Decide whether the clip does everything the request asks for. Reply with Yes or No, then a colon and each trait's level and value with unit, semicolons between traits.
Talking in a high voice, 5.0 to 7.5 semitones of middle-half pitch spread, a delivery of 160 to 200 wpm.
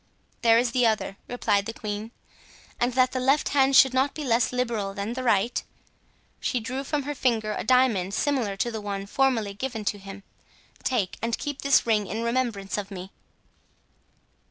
No: high, 230 Hz; average, 3.9 semitones; average, 180 wpm